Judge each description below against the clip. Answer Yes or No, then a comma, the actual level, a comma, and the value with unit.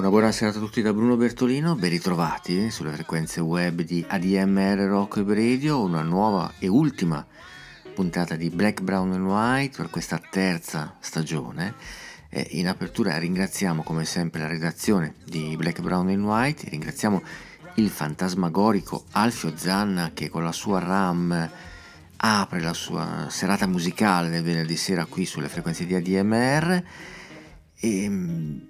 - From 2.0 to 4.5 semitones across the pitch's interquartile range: Yes, average, 3.9 semitones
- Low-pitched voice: Yes, very low, 90 Hz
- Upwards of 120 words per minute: Yes, average, 140 wpm